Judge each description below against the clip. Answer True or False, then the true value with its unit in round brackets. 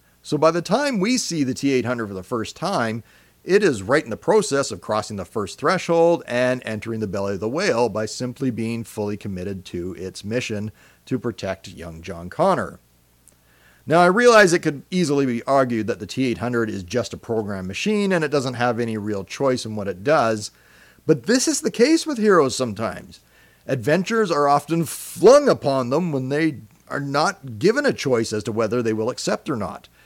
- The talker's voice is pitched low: True (120 Hz)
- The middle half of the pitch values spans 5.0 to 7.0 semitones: True (5.6 semitones)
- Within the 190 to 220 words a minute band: True (200 wpm)